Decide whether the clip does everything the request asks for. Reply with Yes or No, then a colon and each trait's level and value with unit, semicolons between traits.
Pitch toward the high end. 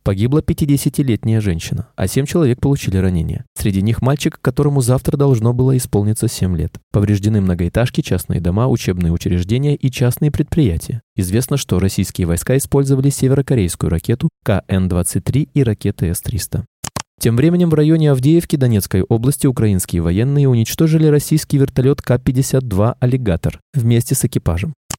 No: low, 125 Hz